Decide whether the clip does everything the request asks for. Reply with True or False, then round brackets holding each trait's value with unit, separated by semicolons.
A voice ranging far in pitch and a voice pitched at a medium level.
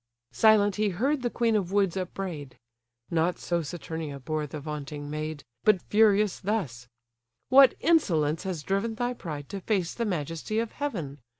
True (5.9 semitones; 180 Hz)